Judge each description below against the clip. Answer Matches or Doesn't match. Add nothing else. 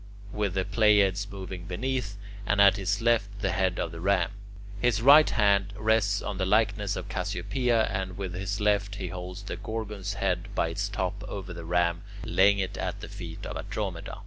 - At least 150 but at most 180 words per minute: Doesn't match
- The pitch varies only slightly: Matches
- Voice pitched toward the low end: Matches